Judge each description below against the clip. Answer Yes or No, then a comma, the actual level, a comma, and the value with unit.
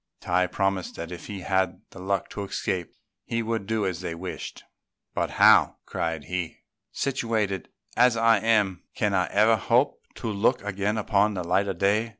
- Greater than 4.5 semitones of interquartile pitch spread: No, average, 3.2 semitones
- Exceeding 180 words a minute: No, average, 175 wpm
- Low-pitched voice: Yes, low, 100 Hz